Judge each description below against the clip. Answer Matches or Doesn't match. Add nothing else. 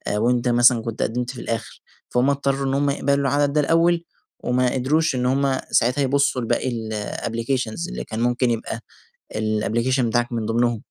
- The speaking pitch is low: Matches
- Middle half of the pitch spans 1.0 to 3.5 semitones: Matches